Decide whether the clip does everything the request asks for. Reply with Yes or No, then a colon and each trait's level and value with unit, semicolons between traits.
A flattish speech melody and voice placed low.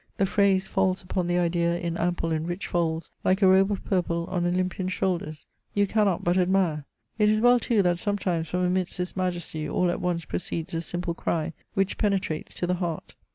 No: narrow, 2.0 semitones; medium, 180 Hz